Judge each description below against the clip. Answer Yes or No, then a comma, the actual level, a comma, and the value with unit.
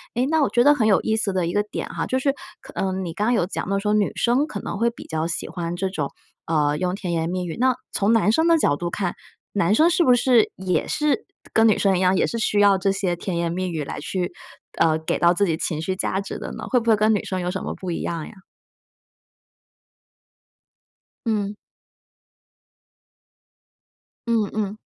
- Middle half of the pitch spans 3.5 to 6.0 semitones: Yes, average, 4.1 semitones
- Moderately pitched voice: No, high, 195 Hz